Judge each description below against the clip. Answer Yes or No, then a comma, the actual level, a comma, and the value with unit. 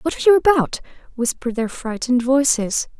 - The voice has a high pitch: Yes, very high, 265 Hz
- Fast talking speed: No, average, 160 wpm